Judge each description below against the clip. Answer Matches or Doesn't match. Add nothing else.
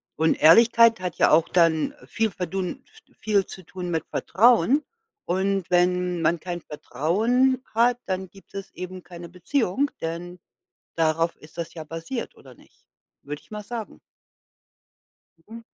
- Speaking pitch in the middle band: Matches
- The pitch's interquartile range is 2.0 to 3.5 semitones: Doesn't match